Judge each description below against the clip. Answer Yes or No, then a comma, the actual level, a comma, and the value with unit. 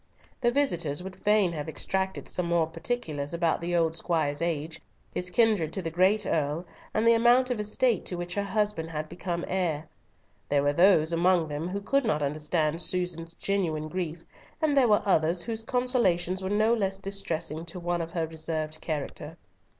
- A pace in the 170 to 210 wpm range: Yes, average, 180 wpm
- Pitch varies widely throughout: No, average, 4.0 semitones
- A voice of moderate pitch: Yes, medium, 175 Hz